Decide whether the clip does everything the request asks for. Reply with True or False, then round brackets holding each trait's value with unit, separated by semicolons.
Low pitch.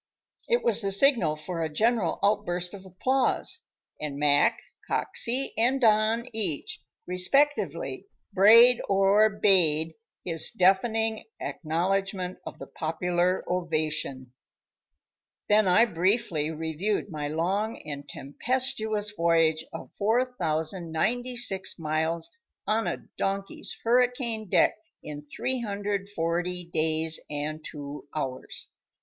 False (185 Hz)